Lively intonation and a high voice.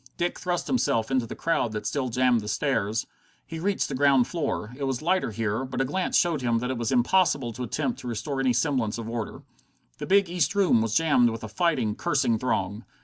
No: wide, 6.0 semitones; low, 130 Hz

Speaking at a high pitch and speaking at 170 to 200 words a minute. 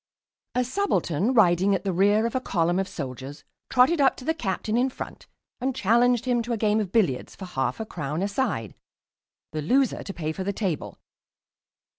Yes: high, 205 Hz; average, 195 wpm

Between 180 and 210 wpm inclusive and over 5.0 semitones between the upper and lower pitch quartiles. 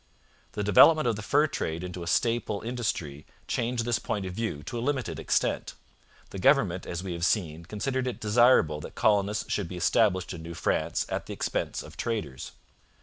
Yes: average, 190 wpm; wide, 5.5 semitones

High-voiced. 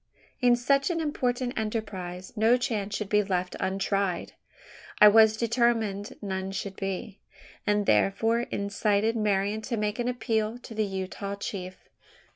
Yes: high, 210 Hz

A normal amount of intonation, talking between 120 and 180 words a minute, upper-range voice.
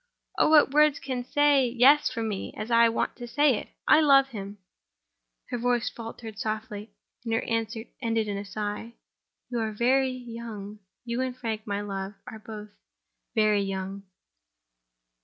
Yes: average, 3.2 semitones; average, 160 wpm; high, 230 Hz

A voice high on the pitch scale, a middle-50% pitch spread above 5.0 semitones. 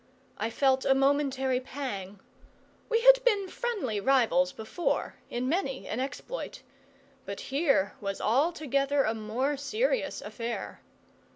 Yes: very high, 270 Hz; wide, 5.4 semitones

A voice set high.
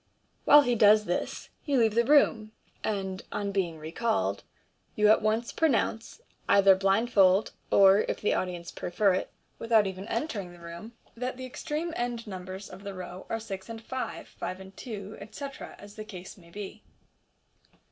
Yes: high, 205 Hz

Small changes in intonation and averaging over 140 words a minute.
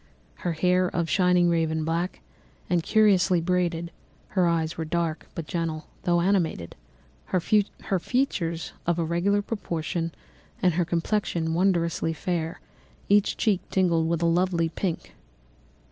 No: narrow, 2.0 semitones; slow, 135 wpm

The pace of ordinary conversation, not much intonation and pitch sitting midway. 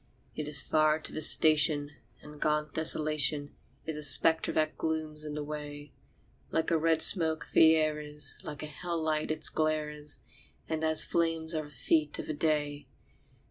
Yes: average, 180 wpm; narrow, 1.0 semitones; medium, 155 Hz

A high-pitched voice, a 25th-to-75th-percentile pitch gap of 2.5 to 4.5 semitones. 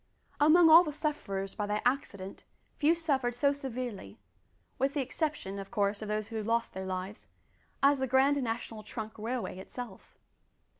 No: high, 240 Hz; average, 5.3 semitones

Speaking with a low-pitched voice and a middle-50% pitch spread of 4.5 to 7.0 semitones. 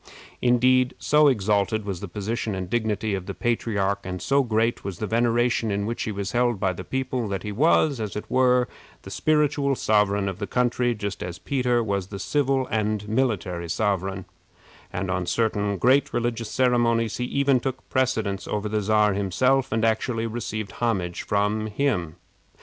No: low, 110 Hz; average, 3.7 semitones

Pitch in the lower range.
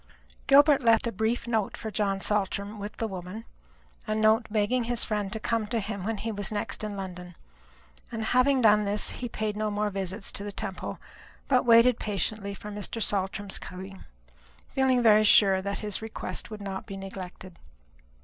No: high, 210 Hz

